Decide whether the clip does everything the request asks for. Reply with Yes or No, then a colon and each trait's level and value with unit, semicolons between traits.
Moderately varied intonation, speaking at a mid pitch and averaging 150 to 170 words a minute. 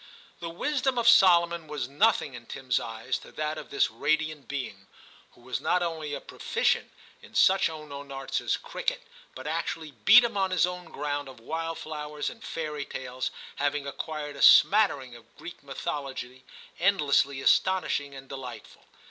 Yes: average, 4.4 semitones; medium, 150 Hz; average, 165 wpm